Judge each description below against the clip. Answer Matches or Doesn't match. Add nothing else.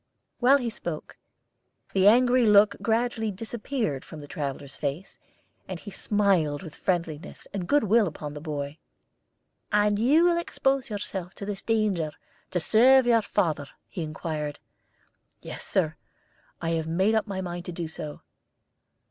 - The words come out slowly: Doesn't match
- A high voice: Matches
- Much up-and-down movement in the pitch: Matches